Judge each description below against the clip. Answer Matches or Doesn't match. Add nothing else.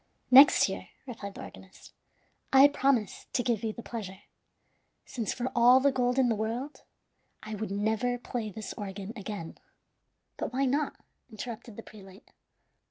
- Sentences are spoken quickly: Doesn't match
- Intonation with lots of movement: Doesn't match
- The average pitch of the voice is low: Doesn't match